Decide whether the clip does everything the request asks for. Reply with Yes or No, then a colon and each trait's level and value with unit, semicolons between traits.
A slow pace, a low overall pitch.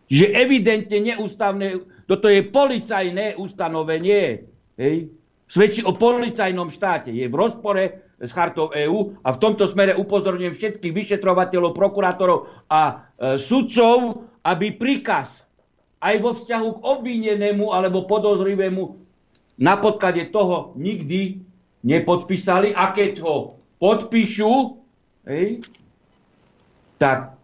No: slow, 105 wpm; high, 195 Hz